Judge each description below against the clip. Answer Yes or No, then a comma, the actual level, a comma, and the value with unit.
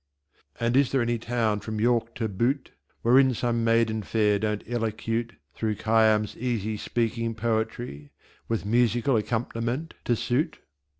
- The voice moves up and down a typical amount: No, narrow, 1.7 semitones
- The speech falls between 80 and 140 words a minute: Yes, slow, 135 wpm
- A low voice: Yes, low, 115 Hz